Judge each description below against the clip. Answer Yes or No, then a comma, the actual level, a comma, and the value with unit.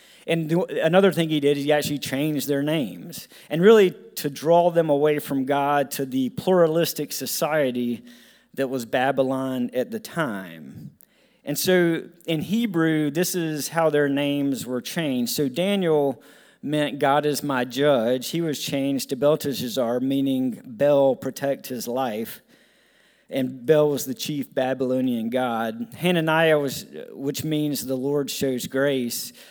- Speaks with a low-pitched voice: No, medium, 145 Hz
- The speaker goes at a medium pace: Yes, average, 145 wpm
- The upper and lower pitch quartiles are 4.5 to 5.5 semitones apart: No, average, 3.7 semitones